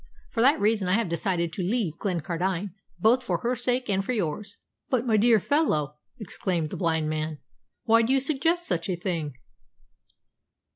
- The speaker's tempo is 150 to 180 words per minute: Yes, average, 175 wpm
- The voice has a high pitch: Yes, high, 195 Hz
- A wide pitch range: Yes, wide, 6.0 semitones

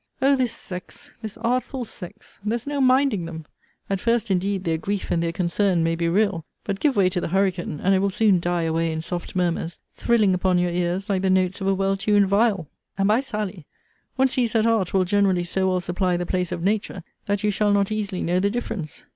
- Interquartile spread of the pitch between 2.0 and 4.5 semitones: Yes, average, 3.2 semitones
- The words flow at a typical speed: No, fast, 225 wpm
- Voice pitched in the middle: No, high, 195 Hz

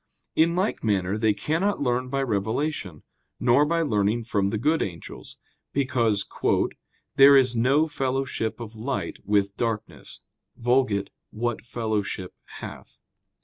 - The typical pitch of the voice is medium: No, low, 120 Hz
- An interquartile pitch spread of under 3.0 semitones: No, average, 4.7 semitones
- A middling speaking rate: No, slow, 125 wpm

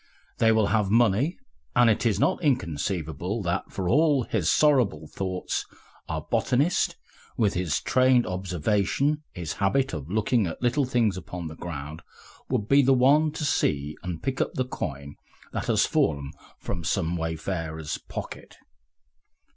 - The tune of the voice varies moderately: No, wide, 7.6 semitones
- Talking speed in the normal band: Yes, average, 150 wpm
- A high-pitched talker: No, low, 100 Hz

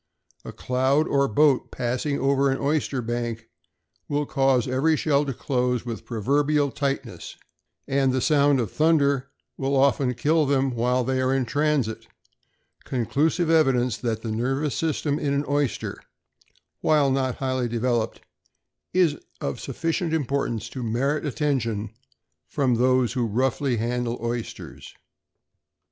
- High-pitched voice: No, low, 135 Hz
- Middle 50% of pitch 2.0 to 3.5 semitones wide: Yes, average, 2.9 semitones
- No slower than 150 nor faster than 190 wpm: No, slow, 135 wpm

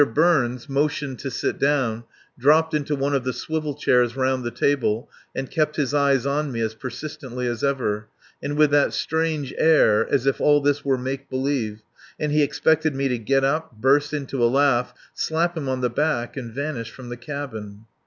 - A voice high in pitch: No, low, 135 Hz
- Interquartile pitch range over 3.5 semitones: No, average, 3.1 semitones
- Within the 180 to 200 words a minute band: Yes, average, 195 wpm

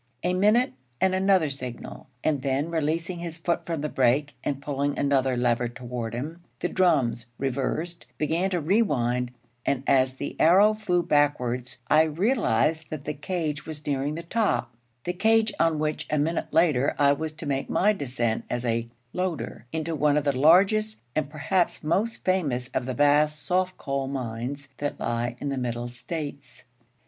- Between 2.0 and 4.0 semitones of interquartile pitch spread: No, average, 4.5 semitones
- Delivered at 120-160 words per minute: No, average, 170 wpm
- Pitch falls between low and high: Yes, medium, 150 Hz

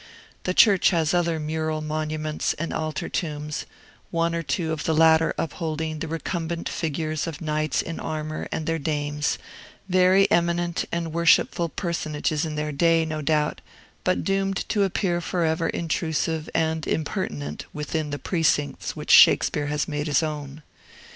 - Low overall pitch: No, medium, 160 Hz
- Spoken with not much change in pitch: Yes, narrow, 1.8 semitones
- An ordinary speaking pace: Yes, average, 150 wpm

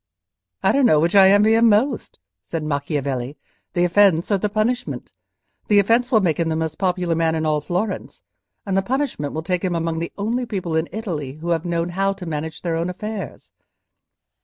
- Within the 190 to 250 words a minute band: Yes, average, 200 wpm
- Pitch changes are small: No, average, 4.2 semitones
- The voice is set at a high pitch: No, medium, 175 Hz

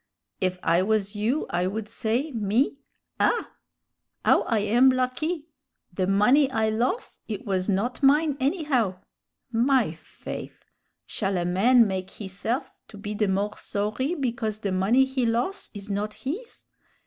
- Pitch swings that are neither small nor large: Yes, average, 4.6 semitones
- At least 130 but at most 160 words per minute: Yes, average, 150 wpm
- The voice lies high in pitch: Yes, high, 220 Hz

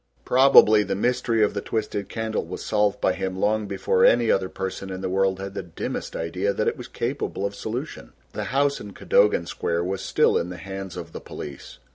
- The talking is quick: Yes, fast, 210 wpm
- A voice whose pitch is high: No, low, 100 Hz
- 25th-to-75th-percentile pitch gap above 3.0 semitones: No, average, 2.7 semitones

